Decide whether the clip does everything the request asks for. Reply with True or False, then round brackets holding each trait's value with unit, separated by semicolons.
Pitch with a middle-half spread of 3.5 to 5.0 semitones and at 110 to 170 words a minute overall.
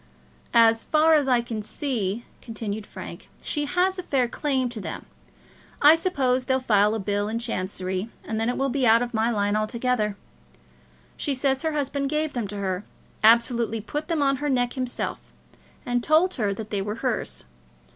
False (4.5 semitones; 185 wpm)